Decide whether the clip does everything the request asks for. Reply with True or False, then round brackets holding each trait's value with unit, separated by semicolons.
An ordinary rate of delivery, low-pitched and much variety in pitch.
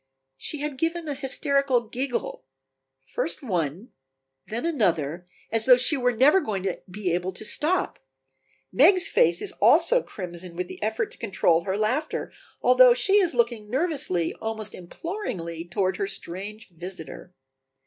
False (150 wpm; 225 Hz; 7.5 semitones)